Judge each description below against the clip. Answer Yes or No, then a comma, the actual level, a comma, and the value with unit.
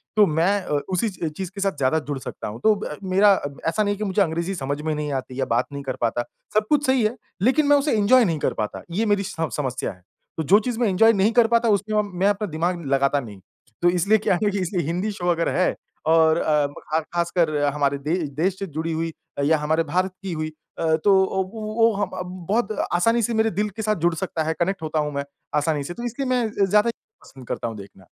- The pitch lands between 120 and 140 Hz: No, medium, 175 Hz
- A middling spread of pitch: No, wide, 5.7 semitones